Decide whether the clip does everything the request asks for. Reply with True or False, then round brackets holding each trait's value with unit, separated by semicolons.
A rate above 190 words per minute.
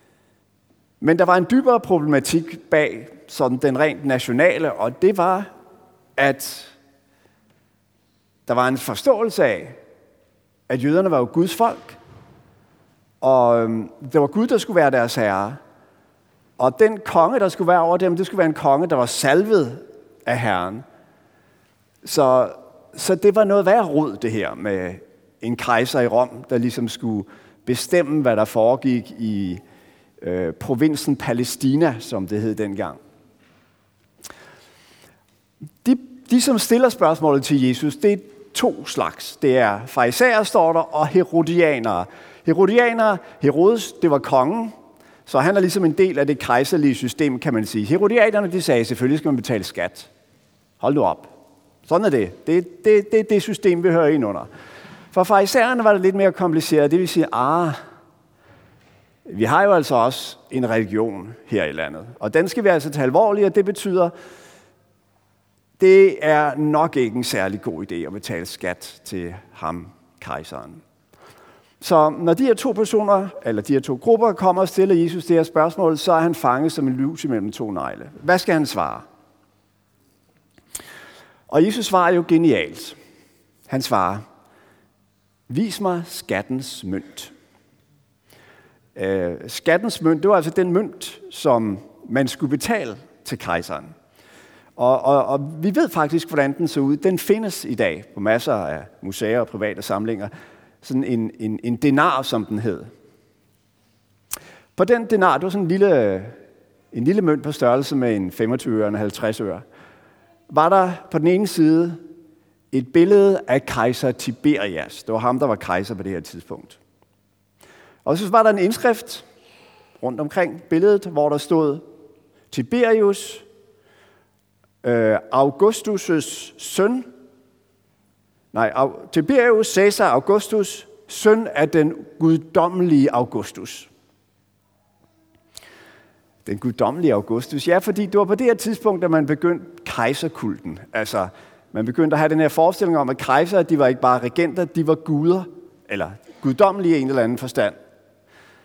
False (155 wpm)